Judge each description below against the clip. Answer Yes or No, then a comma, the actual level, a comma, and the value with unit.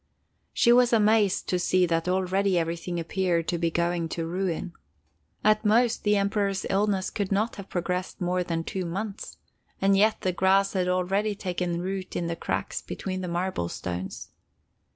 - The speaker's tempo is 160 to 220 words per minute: Yes, average, 170 wpm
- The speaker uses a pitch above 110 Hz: Yes, medium, 185 Hz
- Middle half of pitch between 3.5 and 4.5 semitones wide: No, narrow, 2.4 semitones